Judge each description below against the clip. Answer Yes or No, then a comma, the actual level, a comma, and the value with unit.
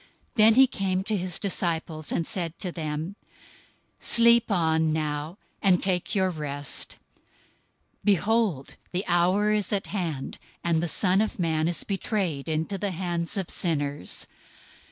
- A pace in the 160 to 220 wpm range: No, average, 145 wpm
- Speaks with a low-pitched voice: No, medium, 175 Hz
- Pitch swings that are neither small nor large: Yes, average, 3.8 semitones